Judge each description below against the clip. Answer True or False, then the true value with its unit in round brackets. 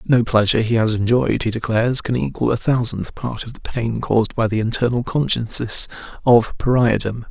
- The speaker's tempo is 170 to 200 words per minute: True (180 wpm)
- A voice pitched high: False (115 Hz)